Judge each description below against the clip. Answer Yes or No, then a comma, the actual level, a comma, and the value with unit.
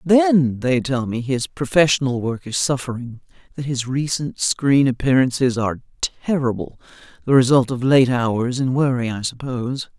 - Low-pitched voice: Yes, low, 130 Hz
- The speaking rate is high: No, average, 150 wpm